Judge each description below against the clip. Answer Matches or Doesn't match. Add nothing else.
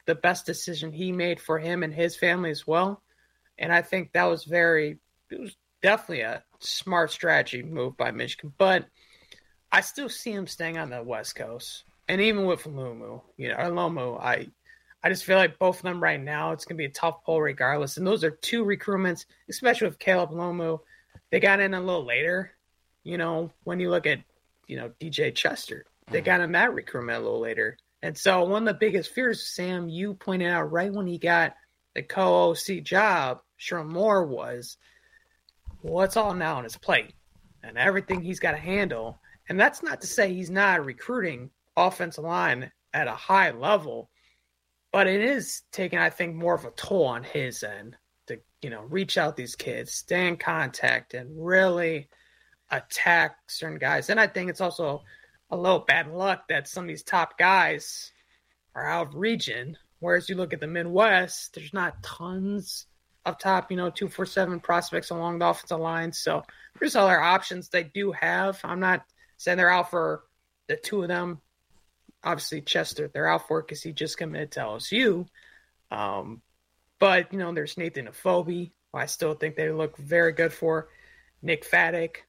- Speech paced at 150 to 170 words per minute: Doesn't match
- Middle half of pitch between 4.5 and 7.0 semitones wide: Doesn't match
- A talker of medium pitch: Matches